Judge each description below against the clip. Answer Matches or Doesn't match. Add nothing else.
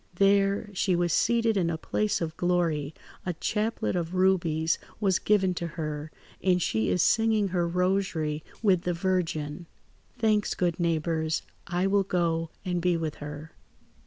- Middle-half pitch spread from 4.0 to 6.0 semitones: Doesn't match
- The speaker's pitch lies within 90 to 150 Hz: Doesn't match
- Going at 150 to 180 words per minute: Matches